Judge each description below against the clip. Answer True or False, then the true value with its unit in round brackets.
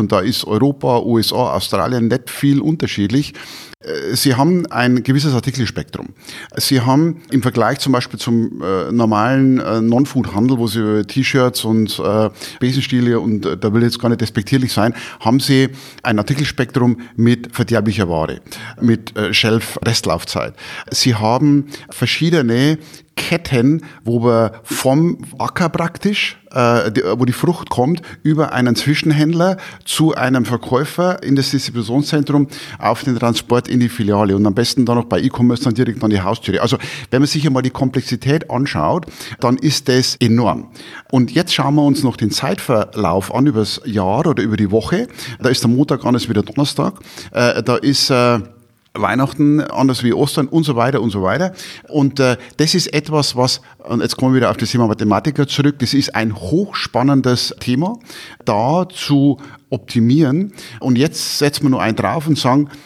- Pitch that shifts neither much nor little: True (3.7 semitones)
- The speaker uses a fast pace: False (165 wpm)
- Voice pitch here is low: True (125 Hz)